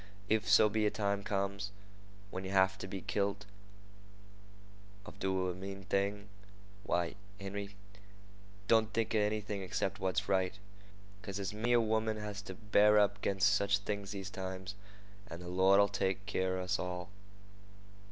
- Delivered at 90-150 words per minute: No, average, 160 wpm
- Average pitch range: No, narrow, 1.7 semitones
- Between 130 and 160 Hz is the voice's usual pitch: No, low, 100 Hz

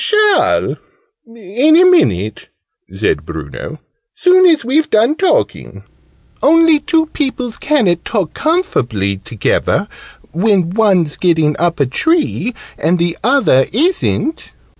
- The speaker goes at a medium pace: No, slow, 115 wpm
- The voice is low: No, high, 225 Hz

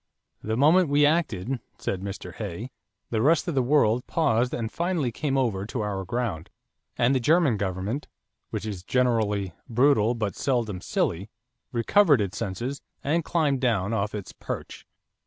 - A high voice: No, low, 120 Hz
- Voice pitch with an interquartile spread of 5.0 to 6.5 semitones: Yes, wide, 5.5 semitones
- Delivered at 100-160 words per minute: Yes, average, 155 wpm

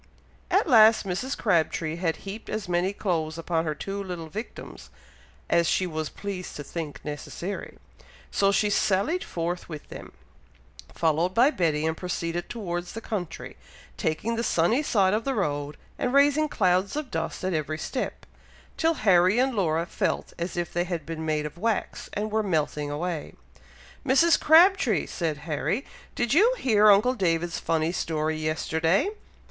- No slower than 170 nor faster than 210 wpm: No, average, 160 wpm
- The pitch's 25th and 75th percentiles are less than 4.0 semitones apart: No, average, 5.2 semitones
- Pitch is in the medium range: Yes, medium, 180 Hz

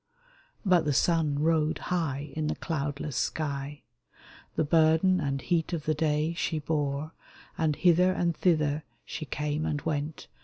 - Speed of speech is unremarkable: Yes, average, 150 wpm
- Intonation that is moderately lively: No, narrow, 2.0 semitones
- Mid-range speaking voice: Yes, medium, 155 Hz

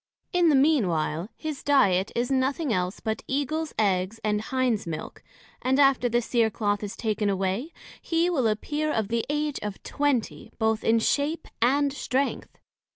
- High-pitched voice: Yes, high, 240 Hz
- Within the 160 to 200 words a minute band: Yes, average, 165 wpm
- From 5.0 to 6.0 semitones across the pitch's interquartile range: Yes, wide, 5.5 semitones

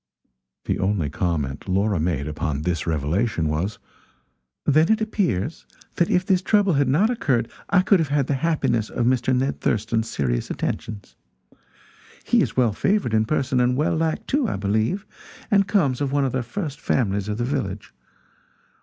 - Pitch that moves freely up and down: Yes, wide, 8.5 semitones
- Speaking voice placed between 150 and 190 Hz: No, low, 125 Hz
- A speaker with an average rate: Yes, average, 170 wpm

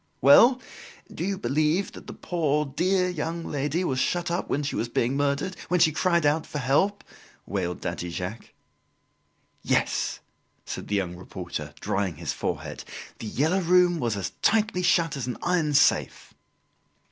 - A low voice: No, medium, 150 Hz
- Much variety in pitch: Yes, wide, 7.1 semitones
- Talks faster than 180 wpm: No, average, 160 wpm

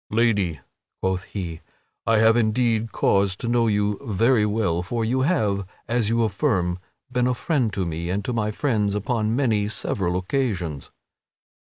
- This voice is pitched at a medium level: No, low, 105 Hz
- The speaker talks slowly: No, average, 160 wpm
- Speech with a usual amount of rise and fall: Yes, average, 3.6 semitones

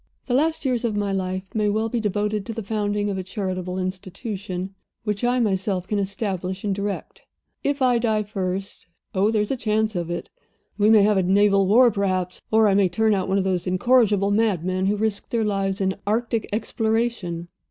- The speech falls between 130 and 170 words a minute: No, average, 200 wpm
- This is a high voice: Yes, high, 205 Hz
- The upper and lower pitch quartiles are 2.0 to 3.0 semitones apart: Yes, narrow, 2.6 semitones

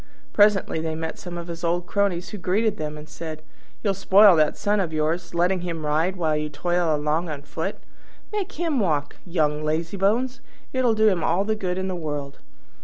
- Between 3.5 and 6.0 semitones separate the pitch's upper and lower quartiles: Yes, average, 4.2 semitones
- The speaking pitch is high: No, medium, 175 Hz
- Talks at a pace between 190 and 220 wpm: Yes, average, 195 wpm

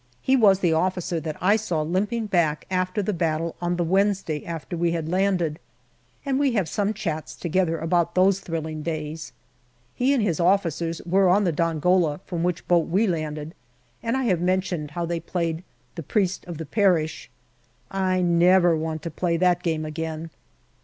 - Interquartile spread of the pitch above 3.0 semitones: No, average, 2.7 semitones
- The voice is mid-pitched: Yes, medium, 175 Hz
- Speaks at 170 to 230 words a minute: Yes, average, 180 wpm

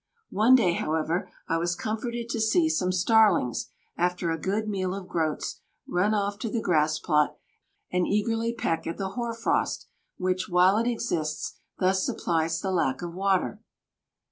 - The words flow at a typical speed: Yes, average, 165 wpm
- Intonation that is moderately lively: Yes, average, 4.3 semitones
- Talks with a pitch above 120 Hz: Yes, medium, 185 Hz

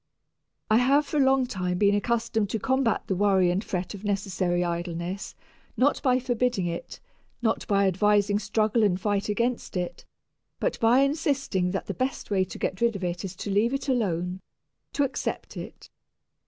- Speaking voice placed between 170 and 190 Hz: No, high, 205 Hz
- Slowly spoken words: No, average, 180 wpm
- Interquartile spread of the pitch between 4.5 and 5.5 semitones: Yes, average, 4.9 semitones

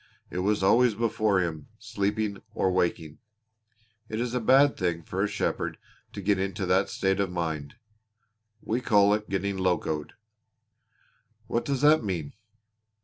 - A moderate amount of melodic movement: Yes, average, 3.2 semitones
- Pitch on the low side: Yes, low, 100 Hz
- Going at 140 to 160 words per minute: Yes, average, 145 wpm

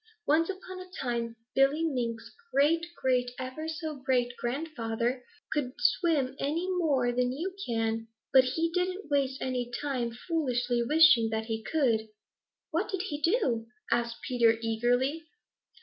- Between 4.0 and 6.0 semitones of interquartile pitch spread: Yes, average, 4.9 semitones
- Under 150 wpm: Yes, average, 140 wpm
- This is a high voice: Yes, very high, 260 Hz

